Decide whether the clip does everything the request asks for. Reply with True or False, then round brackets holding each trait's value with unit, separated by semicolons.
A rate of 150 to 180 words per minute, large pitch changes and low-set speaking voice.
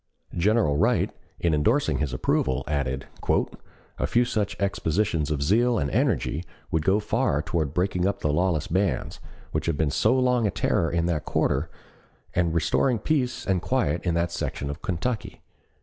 True (165 wpm; 5.9 semitones; 85 Hz)